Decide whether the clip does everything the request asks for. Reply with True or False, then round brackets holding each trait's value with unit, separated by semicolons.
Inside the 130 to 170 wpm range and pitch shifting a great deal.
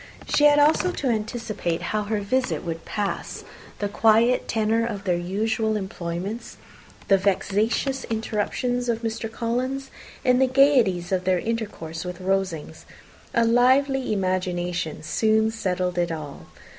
False (135 wpm; 4.4 semitones)